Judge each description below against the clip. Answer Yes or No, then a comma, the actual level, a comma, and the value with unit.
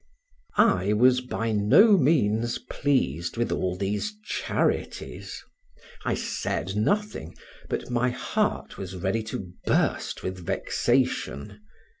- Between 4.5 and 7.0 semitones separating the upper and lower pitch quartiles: Yes, average, 5.1 semitones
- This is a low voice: Yes, low, 105 Hz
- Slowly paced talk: Yes, slow, 110 wpm